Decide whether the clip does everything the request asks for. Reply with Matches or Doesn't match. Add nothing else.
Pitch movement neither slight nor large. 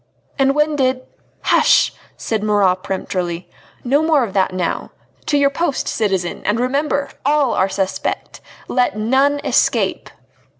Doesn't match